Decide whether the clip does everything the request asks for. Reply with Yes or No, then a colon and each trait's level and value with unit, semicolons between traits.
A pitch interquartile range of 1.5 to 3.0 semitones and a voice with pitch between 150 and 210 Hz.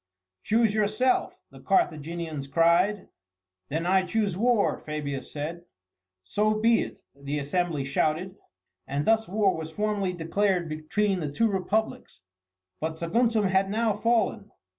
No: average, 5.0 semitones; medium, 185 Hz